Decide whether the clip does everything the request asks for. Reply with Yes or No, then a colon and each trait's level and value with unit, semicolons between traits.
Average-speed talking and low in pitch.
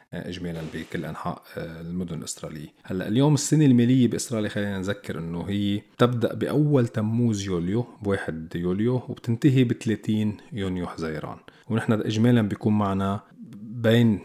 Yes: average, 120 wpm; low, 105 Hz